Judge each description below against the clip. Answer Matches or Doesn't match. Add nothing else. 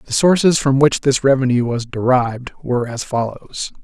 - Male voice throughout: Matches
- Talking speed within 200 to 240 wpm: Doesn't match